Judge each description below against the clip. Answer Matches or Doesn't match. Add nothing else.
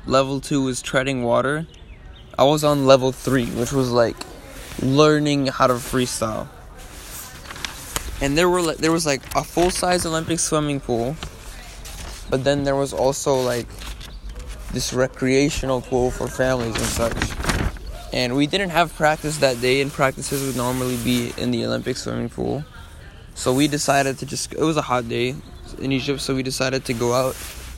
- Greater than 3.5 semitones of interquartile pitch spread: Doesn't match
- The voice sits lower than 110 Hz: Doesn't match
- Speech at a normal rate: Matches